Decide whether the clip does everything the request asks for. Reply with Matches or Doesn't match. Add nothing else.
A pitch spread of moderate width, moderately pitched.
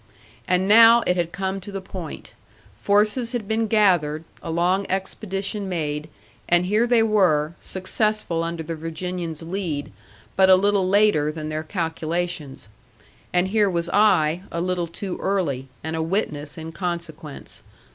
Matches